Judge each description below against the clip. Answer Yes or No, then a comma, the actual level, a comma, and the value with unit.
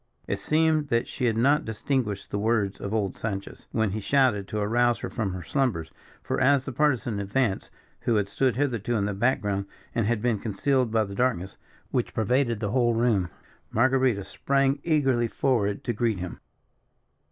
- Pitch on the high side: No, low, 115 Hz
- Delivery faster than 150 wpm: Yes, average, 185 wpm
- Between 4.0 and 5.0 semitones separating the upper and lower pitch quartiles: Yes, average, 4.3 semitones